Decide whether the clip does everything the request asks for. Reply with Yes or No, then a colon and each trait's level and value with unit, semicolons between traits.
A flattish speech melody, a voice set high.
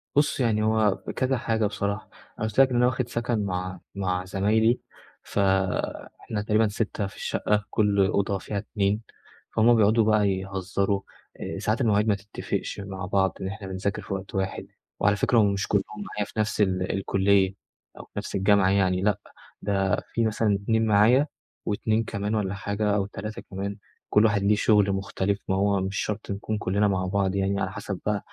No: narrow, 1.8 semitones; low, 100 Hz